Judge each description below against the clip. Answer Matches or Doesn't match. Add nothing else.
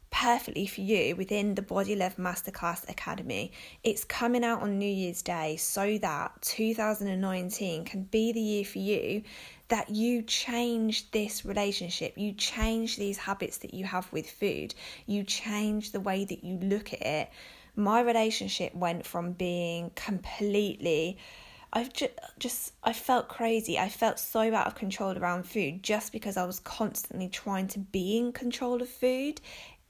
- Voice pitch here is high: Matches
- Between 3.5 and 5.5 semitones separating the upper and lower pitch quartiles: Doesn't match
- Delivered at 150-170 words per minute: Matches